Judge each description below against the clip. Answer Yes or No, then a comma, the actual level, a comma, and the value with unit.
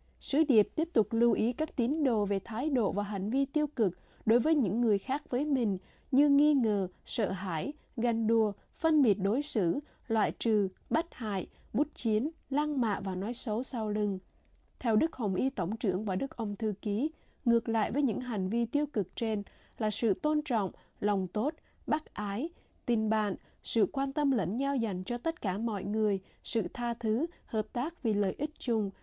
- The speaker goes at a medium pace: Yes, average, 205 wpm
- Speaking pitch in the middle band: No, high, 225 Hz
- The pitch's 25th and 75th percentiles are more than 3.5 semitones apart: Yes, average, 4.7 semitones